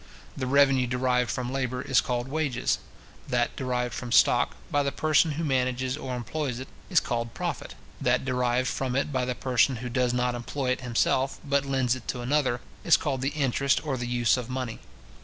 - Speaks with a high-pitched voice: No, low, 130 Hz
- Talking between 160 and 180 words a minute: No, average, 195 wpm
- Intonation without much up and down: Yes, narrow, 1.8 semitones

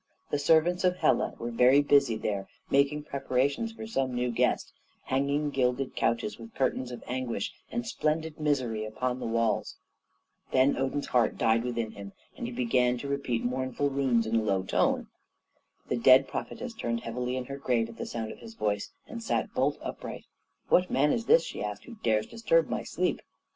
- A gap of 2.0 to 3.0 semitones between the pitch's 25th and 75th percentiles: No, average, 4.0 semitones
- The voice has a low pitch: Yes, low, 130 Hz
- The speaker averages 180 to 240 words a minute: Yes, average, 185 wpm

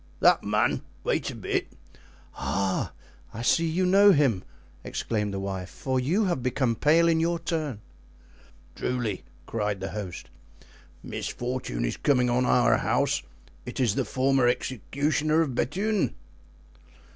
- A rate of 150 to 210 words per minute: No, slow, 135 wpm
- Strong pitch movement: Yes, wide, 6.9 semitones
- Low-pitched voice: Yes, low, 130 Hz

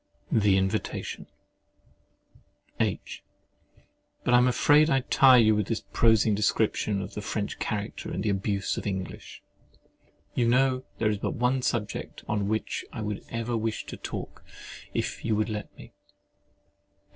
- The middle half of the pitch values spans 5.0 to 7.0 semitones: No, average, 2.8 semitones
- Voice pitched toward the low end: Yes, low, 110 Hz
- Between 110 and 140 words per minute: No, average, 155 wpm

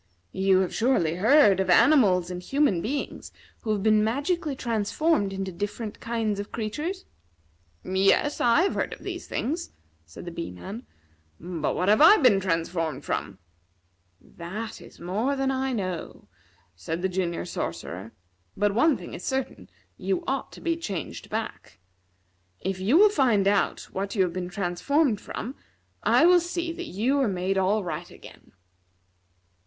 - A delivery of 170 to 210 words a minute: No, average, 160 wpm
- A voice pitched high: Yes, high, 205 Hz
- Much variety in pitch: Yes, wide, 6.7 semitones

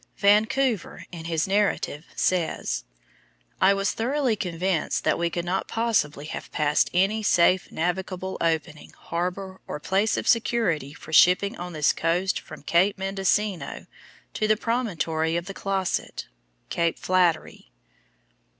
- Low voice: No, medium, 185 Hz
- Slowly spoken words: Yes, slow, 130 wpm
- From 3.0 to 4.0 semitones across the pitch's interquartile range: Yes, average, 3.4 semitones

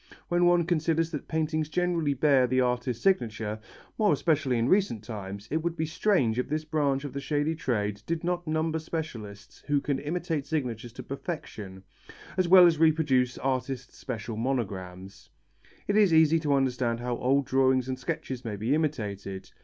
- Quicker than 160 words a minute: Yes, average, 170 wpm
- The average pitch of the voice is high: No, medium, 140 Hz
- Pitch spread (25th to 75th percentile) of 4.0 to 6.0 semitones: Yes, average, 5.0 semitones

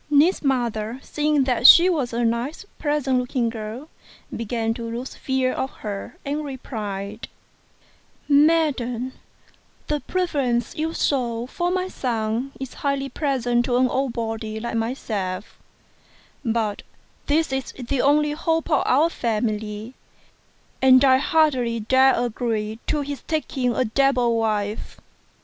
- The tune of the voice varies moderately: Yes, average, 3.8 semitones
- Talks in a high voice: Yes, very high, 250 Hz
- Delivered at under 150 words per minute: Yes, slow, 135 wpm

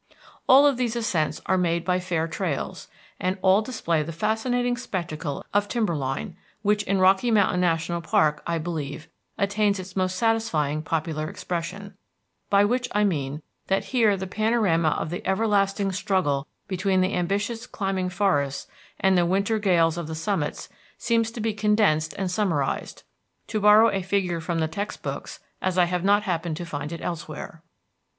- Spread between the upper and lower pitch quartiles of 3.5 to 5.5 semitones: Yes, average, 4.0 semitones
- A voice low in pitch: No, medium, 185 Hz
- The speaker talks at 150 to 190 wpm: Yes, average, 165 wpm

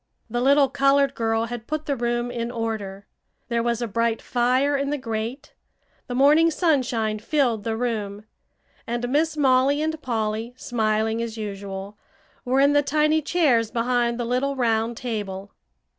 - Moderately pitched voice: No, high, 240 Hz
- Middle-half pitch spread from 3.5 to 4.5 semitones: Yes, average, 3.8 semitones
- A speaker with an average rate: Yes, average, 160 wpm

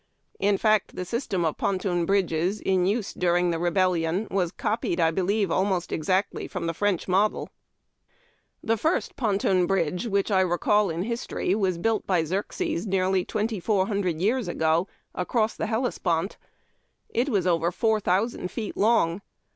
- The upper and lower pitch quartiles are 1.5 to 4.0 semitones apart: Yes, average, 3.3 semitones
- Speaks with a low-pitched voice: No, high, 190 Hz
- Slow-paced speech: No, average, 160 wpm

